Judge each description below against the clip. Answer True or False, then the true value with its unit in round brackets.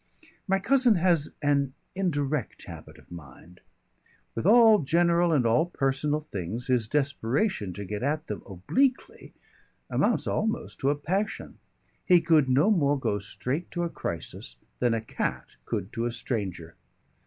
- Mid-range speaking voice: True (145 Hz)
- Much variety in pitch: True (7.4 semitones)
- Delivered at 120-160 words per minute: True (150 wpm)